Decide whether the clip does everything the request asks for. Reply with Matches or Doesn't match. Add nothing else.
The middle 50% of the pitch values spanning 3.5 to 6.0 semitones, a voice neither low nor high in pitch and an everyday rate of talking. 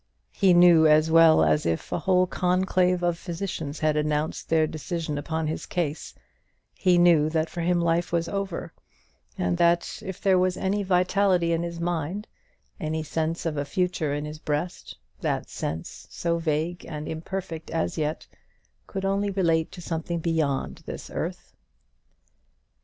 Doesn't match